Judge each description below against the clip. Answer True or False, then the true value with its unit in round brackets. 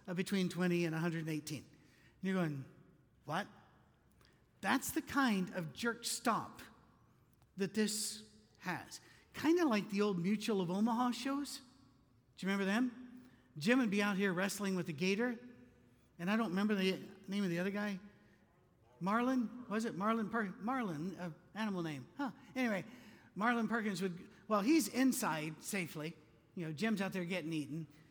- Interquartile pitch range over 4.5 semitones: True (5.0 semitones)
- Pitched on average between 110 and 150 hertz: False (195 Hz)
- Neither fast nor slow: True (160 wpm)